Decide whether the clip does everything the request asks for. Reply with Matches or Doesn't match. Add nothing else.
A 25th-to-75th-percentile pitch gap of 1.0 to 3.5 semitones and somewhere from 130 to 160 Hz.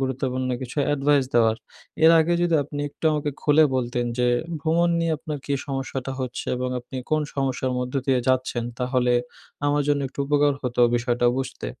Matches